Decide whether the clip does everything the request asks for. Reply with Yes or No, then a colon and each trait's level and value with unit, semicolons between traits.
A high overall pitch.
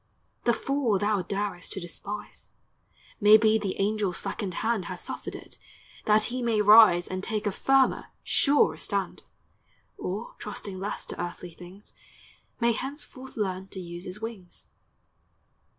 Yes: high, 205 Hz